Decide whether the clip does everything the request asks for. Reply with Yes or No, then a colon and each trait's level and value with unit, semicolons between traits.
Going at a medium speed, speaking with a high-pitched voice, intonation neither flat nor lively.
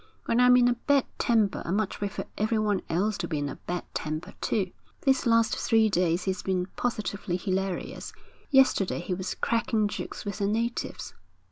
Yes: average, 175 wpm; high, 205 Hz; average, 3.7 semitones